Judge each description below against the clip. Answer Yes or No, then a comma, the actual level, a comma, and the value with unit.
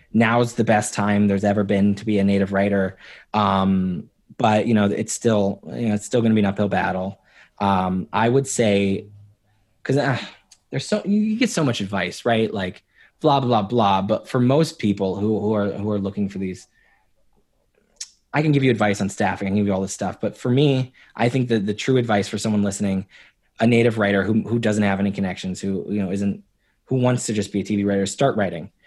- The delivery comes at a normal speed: No, fast, 220 wpm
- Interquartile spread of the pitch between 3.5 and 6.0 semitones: No, average, 2.8 semitones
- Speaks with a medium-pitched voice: No, low, 105 Hz